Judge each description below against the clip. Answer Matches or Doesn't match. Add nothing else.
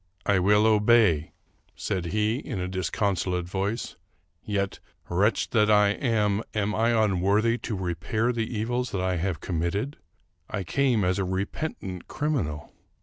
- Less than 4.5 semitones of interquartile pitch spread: Matches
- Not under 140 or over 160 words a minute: Matches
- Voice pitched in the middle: Doesn't match